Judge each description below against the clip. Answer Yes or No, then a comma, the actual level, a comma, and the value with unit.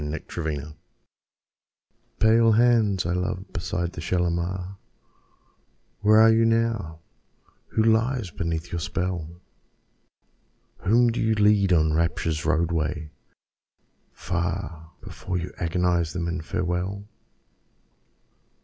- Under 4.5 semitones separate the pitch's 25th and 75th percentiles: Yes, average, 4.1 semitones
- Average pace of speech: No, slow, 105 wpm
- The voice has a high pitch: No, very low, 90 Hz